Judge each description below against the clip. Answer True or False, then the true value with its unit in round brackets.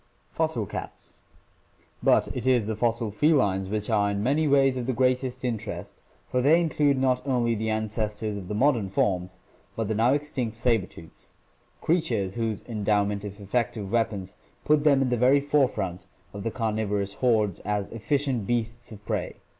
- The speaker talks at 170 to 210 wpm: True (180 wpm)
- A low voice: True (115 Hz)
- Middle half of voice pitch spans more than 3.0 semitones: True (3.9 semitones)